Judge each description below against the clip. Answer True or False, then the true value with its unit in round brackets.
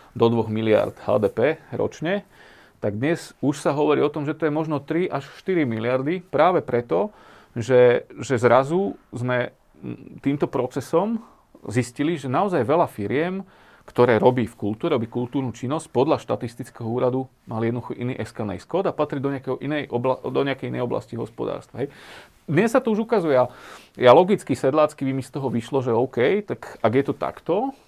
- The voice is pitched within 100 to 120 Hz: False (130 Hz)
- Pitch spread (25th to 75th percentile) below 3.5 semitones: False (4.2 semitones)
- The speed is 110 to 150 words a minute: False (160 wpm)